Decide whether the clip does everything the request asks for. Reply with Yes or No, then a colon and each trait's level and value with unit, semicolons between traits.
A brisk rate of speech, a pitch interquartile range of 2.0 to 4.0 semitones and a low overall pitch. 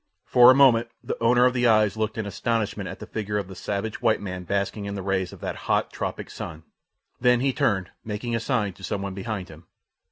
Yes: fast, 230 wpm; average, 3.2 semitones; low, 105 Hz